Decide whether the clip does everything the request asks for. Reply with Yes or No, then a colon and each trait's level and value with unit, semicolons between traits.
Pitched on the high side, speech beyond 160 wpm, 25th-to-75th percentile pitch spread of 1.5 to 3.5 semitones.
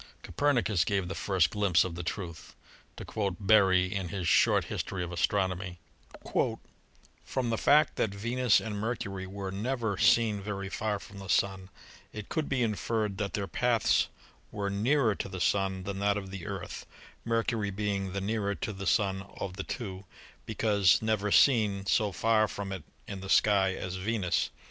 No: low, 100 Hz; average, 170 wpm; narrow, 2.4 semitones